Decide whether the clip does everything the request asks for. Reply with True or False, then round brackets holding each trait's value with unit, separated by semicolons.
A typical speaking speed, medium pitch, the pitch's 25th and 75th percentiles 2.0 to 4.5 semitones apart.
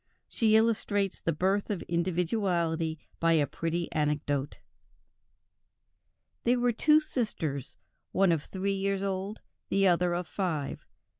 False (125 wpm; 180 Hz; 3.6 semitones)